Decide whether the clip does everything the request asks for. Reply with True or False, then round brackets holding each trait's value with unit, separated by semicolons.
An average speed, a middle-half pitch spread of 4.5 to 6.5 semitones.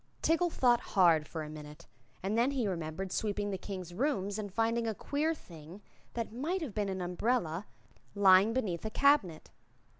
True (180 wpm; 5.1 semitones)